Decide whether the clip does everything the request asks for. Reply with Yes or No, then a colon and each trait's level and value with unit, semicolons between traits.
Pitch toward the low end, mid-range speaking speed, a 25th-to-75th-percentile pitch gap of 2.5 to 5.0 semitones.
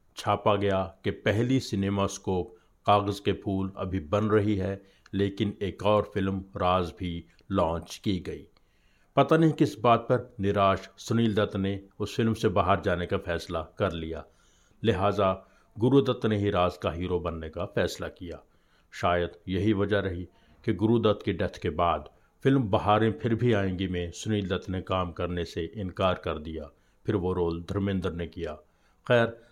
Yes: low, 100 Hz; average, 165 wpm; average, 2.9 semitones